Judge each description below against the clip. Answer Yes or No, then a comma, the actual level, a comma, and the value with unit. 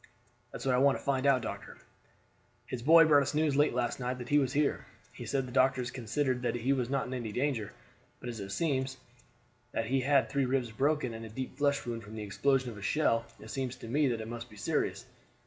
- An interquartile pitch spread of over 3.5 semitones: No, average, 2.9 semitones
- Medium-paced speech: No, fast, 240 wpm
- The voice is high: No, low, 130 Hz